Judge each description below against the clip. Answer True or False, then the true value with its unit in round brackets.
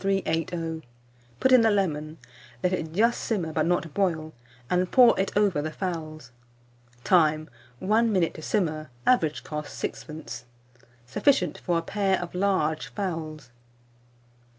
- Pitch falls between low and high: True (170 Hz)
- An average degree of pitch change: True (3.9 semitones)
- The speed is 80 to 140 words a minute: True (135 wpm)